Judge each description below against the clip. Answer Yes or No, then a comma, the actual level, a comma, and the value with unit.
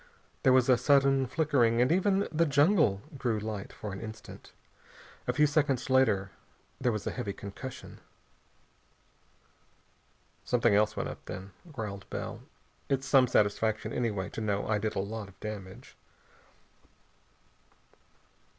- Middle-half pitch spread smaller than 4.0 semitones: No, average, 4.7 semitones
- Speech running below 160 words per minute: Yes, slow, 135 wpm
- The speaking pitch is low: Yes, low, 115 Hz